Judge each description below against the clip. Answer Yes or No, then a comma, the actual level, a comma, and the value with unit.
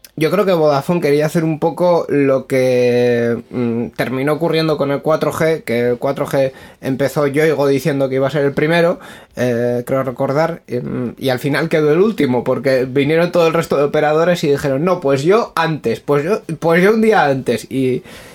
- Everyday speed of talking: No, fast, 195 wpm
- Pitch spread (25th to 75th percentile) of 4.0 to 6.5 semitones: No, average, 3.4 semitones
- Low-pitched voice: No, medium, 145 Hz